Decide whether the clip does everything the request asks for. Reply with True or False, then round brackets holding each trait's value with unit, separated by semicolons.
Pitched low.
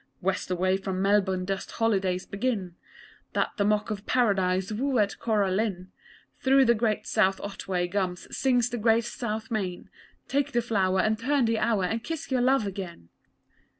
False (210 Hz)